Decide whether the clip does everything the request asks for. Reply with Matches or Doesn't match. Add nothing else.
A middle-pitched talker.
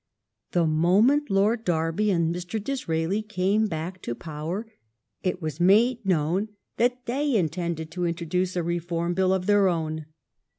Matches